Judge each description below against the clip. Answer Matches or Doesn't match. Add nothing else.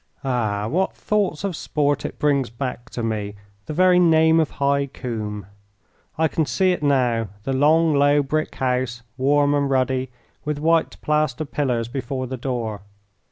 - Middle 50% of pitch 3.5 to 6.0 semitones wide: Matches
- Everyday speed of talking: Matches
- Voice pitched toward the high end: Doesn't match